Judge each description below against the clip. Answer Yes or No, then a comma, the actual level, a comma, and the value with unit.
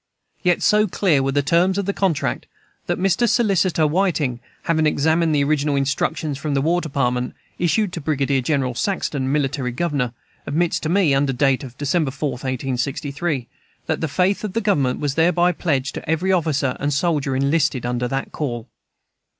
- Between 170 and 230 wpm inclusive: Yes, average, 175 wpm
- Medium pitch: Yes, medium, 150 Hz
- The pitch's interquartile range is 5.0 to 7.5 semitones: No, average, 4.2 semitones